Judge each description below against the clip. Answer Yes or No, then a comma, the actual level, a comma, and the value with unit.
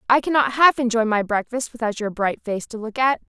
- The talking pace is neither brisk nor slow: No, fast, 230 wpm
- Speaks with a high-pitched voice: Yes, high, 235 Hz